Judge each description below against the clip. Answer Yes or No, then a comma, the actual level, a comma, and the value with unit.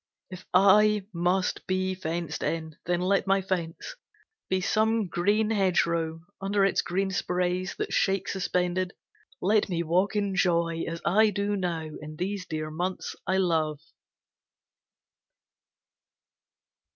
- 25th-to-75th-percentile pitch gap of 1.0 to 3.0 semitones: Yes, narrow, 2.5 semitones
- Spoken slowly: Yes, slow, 125 wpm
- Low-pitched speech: No, medium, 185 Hz